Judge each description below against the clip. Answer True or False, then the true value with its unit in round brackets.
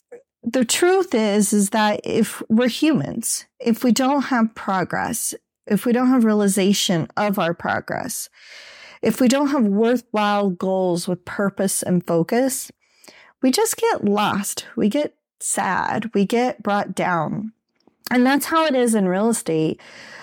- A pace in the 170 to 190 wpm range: False (150 wpm)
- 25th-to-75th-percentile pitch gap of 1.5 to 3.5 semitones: False (4.3 semitones)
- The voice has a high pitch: True (225 Hz)